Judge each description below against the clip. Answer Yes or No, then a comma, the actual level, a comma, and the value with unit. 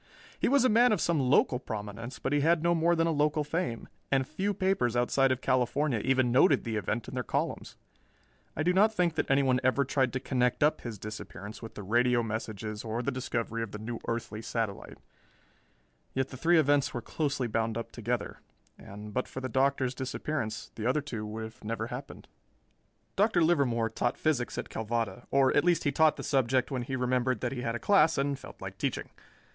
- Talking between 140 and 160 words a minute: No, fast, 205 wpm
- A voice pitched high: No, low, 130 Hz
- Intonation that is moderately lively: Yes, average, 4.2 semitones